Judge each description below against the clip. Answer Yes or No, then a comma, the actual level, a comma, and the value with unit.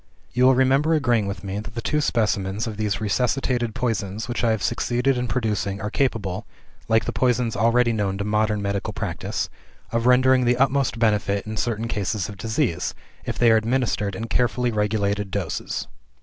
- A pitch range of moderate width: Yes, average, 3.2 semitones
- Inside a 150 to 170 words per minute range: No, average, 180 wpm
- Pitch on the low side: Yes, low, 115 Hz